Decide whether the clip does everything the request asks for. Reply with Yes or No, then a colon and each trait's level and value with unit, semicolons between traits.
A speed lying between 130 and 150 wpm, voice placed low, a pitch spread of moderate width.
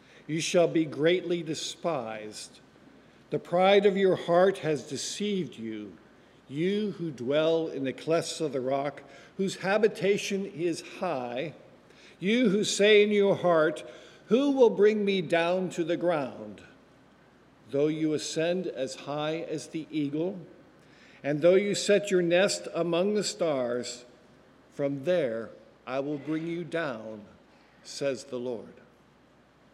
No: slow, 135 wpm; medium, 165 Hz; average, 5.0 semitones